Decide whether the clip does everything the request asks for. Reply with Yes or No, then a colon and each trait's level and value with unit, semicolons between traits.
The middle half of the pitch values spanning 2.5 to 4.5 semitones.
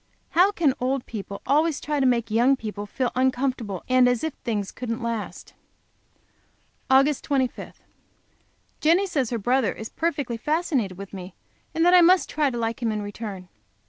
No: average, 4.9 semitones